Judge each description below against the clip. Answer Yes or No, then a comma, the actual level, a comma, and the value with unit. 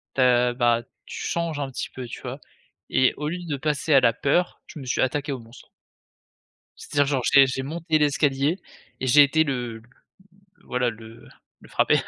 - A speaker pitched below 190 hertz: Yes, low, 135 Hz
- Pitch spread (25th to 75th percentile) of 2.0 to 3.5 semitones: Yes, average, 3.1 semitones